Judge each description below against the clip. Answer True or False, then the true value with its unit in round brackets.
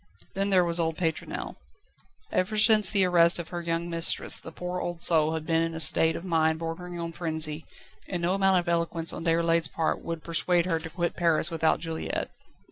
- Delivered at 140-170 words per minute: False (205 wpm)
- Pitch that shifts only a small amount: True (1.5 semitones)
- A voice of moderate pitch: True (170 Hz)